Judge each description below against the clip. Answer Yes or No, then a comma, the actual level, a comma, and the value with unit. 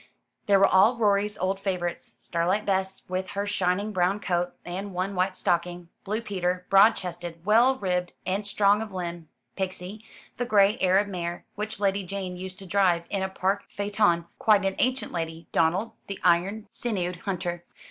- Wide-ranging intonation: No, narrow, 2.4 semitones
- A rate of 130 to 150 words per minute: No, average, 170 wpm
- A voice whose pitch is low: No, high, 190 Hz